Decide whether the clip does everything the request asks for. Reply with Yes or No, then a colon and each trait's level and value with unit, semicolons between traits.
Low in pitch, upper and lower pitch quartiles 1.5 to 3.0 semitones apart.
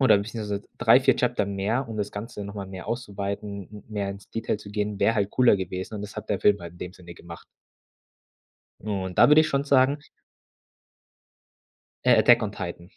Yes: low, 105 Hz; narrow, 2.5 semitones